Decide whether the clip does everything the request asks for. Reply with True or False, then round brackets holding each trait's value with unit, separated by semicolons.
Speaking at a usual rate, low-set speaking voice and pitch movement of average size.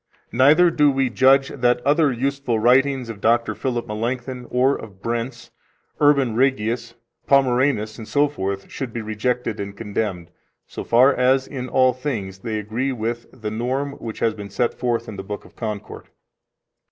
True (160 wpm; 120 Hz; 3.4 semitones)